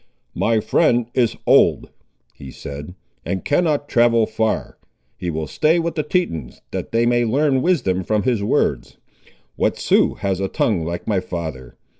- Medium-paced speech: Yes, average, 160 wpm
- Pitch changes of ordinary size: No, wide, 6.5 semitones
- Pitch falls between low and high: No, low, 110 Hz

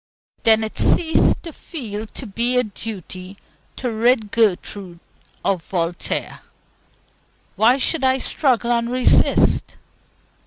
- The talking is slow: Yes, slow, 115 wpm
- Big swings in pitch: No, average, 3.8 semitones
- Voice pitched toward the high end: Yes, high, 225 Hz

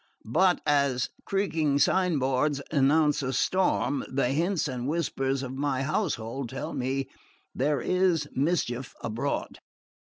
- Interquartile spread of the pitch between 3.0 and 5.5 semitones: Yes, average, 3.5 semitones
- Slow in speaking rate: Yes, slow, 120 wpm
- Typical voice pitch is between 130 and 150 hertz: Yes, medium, 140 Hz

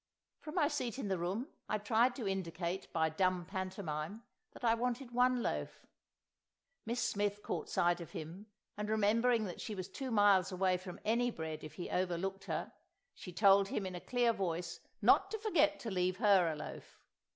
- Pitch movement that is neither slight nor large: Yes, average, 4.5 semitones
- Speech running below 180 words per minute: No, average, 185 wpm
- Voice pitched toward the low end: No, high, 195 Hz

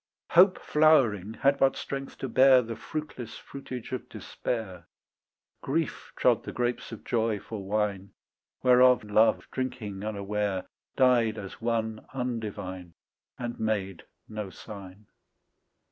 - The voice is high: No, low, 115 Hz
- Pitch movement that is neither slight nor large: Yes, average, 3.7 semitones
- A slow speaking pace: Yes, slow, 120 wpm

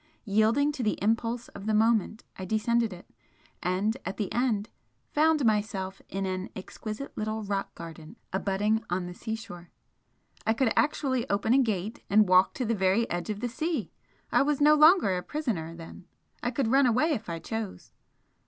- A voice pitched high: Yes, high, 220 Hz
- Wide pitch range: No, average, 4.1 semitones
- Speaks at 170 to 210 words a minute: Yes, average, 180 wpm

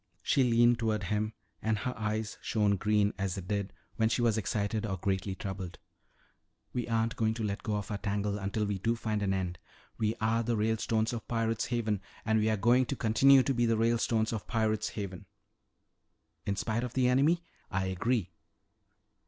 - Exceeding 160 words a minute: Yes, average, 190 wpm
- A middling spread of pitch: No, narrow, 2.3 semitones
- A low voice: Yes, low, 110 Hz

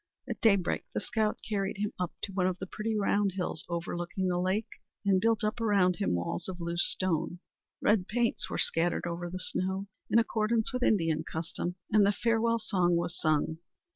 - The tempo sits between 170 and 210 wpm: Yes, average, 190 wpm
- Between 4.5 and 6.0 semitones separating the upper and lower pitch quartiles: No, average, 3.5 semitones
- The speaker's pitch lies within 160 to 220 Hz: Yes, high, 190 Hz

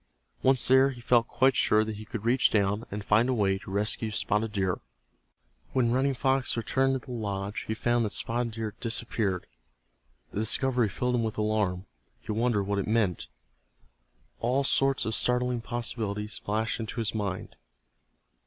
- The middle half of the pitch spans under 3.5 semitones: Yes, average, 2.8 semitones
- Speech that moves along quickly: No, average, 170 wpm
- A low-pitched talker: Yes, low, 115 Hz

